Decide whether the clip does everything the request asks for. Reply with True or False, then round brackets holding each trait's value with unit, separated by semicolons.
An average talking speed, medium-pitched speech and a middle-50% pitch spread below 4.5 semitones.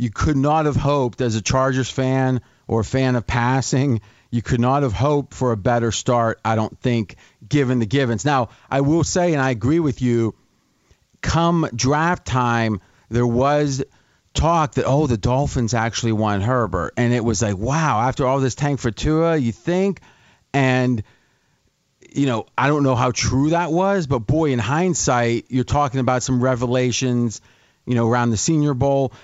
False (180 wpm; 130 Hz; 3.0 semitones)